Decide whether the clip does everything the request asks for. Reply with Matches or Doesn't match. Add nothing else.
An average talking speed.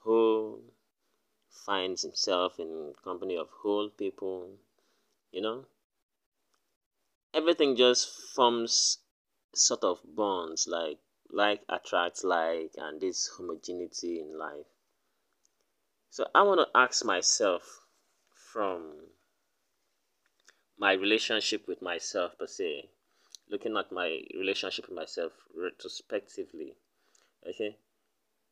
Doesn't match